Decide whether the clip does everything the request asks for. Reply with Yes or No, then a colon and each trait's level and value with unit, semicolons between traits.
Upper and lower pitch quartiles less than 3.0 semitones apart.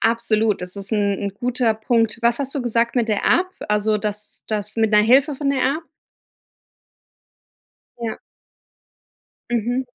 Yes: narrow, 2.6 semitones